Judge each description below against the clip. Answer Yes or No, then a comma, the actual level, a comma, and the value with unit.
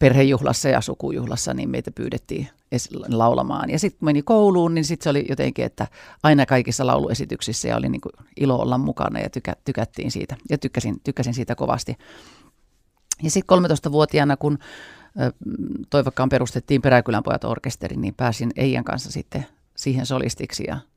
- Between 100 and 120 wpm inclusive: No, average, 140 wpm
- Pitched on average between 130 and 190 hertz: Yes, low, 135 Hz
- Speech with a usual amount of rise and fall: Yes, average, 3.5 semitones